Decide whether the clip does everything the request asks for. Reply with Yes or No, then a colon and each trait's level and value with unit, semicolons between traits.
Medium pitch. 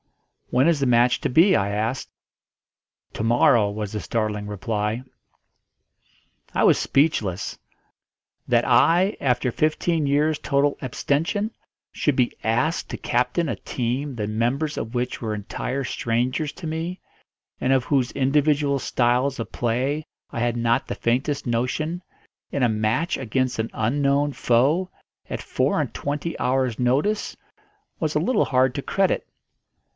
No: low, 130 Hz